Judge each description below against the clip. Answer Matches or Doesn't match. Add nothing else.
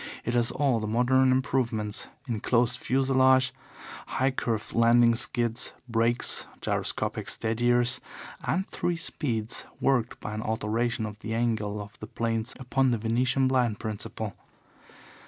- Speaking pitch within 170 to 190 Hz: Doesn't match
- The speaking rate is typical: Doesn't match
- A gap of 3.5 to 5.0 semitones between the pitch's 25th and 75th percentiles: Doesn't match